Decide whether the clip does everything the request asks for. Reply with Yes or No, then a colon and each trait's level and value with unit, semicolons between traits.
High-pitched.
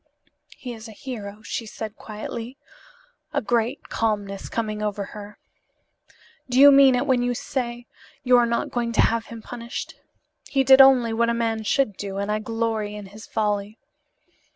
Yes: high, 230 Hz